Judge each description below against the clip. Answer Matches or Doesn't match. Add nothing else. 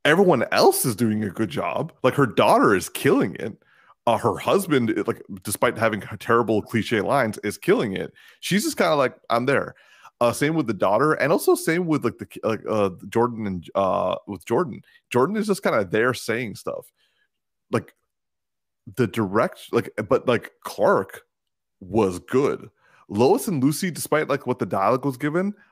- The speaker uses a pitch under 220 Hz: Matches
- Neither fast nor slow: Matches